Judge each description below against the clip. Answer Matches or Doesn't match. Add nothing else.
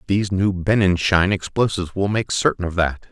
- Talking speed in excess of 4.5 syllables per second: Matches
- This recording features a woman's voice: Doesn't match